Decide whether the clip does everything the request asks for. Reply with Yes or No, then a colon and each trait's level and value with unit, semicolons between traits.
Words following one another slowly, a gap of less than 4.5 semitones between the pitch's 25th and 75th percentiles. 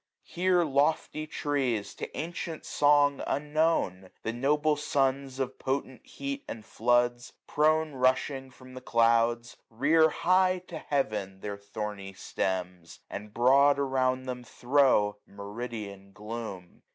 No: slow, 120 wpm; average, 5.2 semitones